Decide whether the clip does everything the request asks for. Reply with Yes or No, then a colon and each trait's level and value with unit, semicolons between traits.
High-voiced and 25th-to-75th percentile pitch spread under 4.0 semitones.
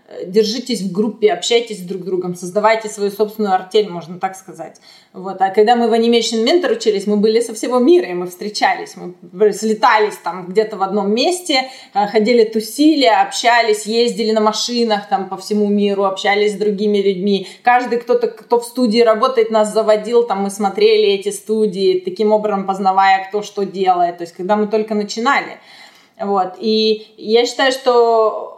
Yes: high, 215 Hz; average, 3.1 semitones